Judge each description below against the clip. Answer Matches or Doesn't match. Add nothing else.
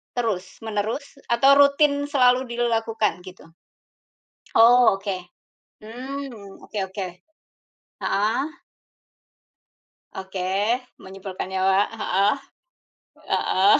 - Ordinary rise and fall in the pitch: Matches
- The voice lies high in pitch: Matches